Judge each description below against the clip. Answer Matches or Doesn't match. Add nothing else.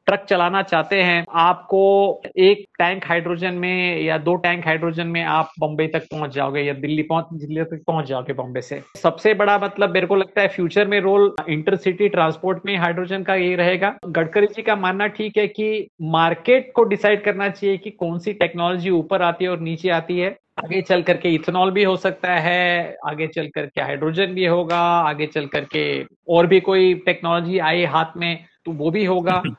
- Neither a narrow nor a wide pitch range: Matches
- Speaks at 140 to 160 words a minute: Doesn't match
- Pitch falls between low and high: Matches